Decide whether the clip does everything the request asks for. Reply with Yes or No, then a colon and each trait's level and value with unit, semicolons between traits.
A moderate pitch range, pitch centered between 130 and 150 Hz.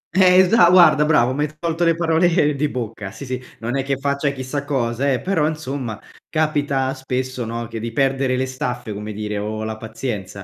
Yes: average, 4.3 semitones; low, 135 Hz